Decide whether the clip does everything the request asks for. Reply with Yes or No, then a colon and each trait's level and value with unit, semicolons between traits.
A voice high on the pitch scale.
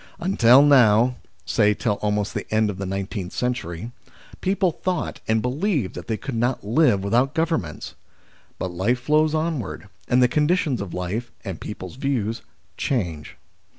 No: low, 120 Hz